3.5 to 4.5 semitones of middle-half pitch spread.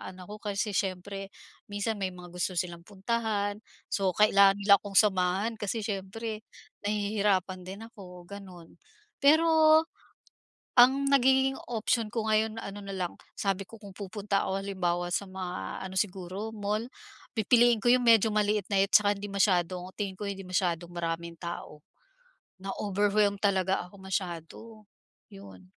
No: narrow, 2.6 semitones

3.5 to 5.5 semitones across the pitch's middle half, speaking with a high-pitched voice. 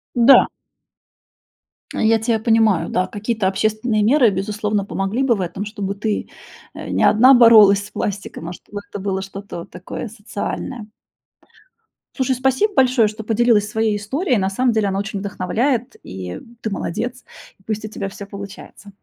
No: average, 2.8 semitones; high, 215 Hz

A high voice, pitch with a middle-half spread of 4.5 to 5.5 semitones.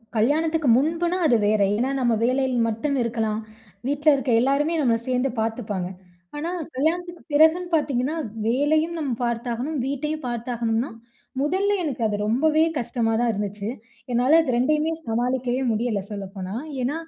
Yes: very high, 255 Hz; average, 4.9 semitones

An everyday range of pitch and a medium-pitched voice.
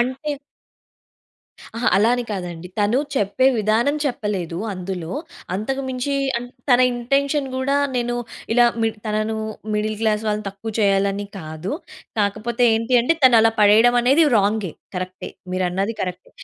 No: average, 3.7 semitones; high, 220 Hz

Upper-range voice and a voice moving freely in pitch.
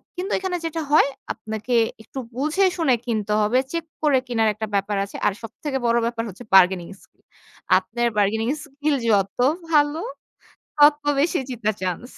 Yes: high, 240 Hz; wide, 6.0 semitones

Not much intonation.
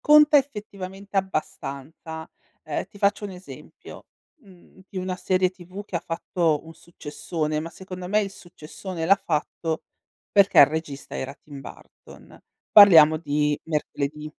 No: average, 4.1 semitones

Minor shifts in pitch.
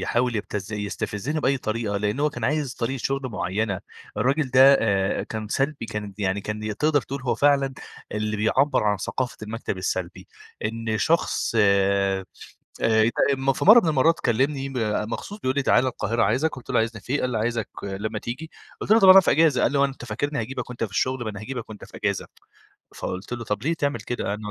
No: average, 4.5 semitones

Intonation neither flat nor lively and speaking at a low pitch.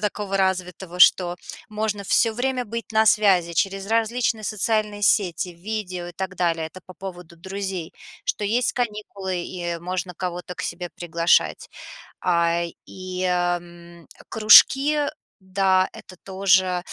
No: average, 3.0 semitones; high, 190 Hz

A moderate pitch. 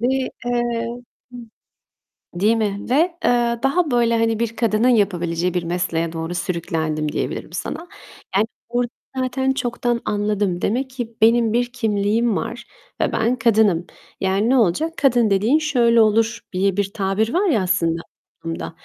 No: high, 225 Hz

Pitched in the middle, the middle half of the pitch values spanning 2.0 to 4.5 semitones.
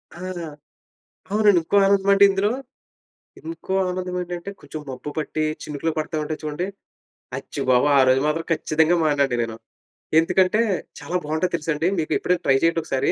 Yes: medium, 165 Hz; average, 3.3 semitones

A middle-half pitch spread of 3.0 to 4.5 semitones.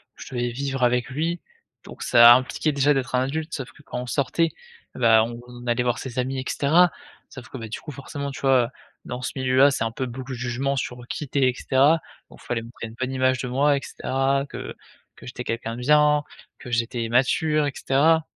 No: narrow, 2.4 semitones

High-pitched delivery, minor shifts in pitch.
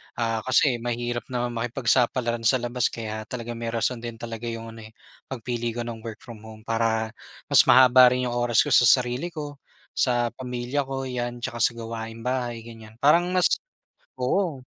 No: low, 120 Hz; narrow, 1.7 semitones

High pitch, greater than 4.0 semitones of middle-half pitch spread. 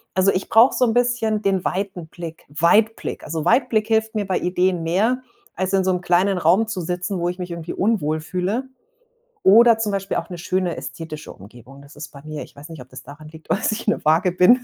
No: medium, 180 Hz; average, 4.7 semitones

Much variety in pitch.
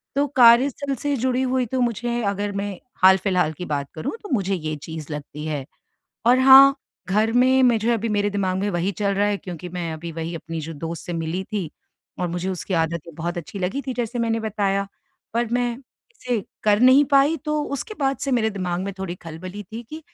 Yes: wide, 6.0 semitones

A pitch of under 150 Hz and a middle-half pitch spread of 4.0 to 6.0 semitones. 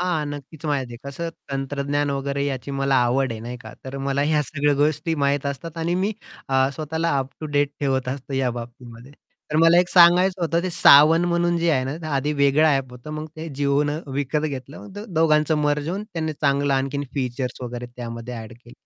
No: medium, 140 Hz; average, 2.8 semitones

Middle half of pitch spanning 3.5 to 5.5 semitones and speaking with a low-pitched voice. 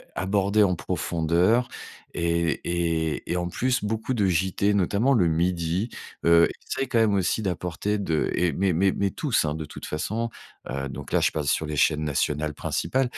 Yes: average, 4.2 semitones; very low, 90 Hz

